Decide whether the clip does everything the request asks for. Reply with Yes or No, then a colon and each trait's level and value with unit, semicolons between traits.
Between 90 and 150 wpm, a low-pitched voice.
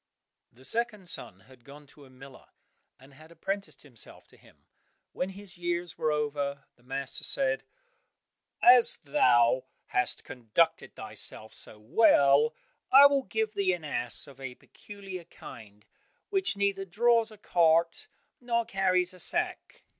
No: average, 140 wpm; medium, 165 Hz